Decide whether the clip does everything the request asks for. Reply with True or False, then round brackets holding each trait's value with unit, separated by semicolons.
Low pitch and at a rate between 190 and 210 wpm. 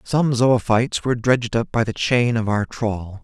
True (115 Hz; 205 wpm)